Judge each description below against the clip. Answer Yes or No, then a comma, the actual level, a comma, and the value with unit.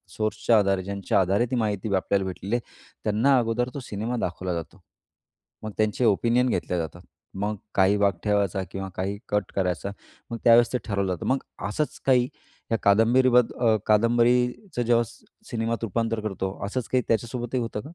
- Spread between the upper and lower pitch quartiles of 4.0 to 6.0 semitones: No, average, 3.4 semitones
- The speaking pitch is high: No, low, 110 Hz